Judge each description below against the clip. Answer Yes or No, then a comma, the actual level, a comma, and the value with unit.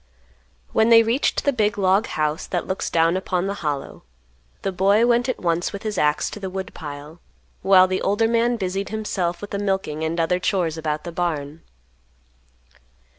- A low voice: No, medium, 185 Hz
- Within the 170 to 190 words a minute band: Yes, average, 180 wpm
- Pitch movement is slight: No, average, 3.9 semitones